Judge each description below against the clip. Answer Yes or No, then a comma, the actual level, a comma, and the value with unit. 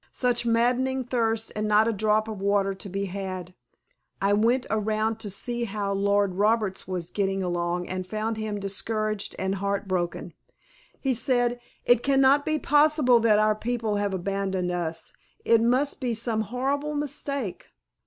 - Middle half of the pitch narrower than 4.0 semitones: Yes, average, 3.6 semitones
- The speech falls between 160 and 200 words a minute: Yes, average, 165 wpm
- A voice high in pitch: Yes, high, 215 Hz